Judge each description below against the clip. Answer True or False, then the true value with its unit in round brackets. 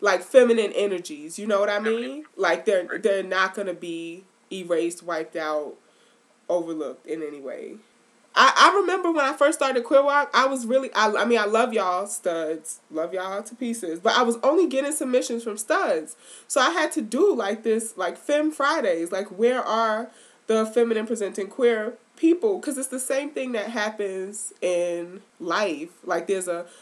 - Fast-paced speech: False (185 wpm)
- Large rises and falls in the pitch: True (6.0 semitones)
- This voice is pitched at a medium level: False (220 Hz)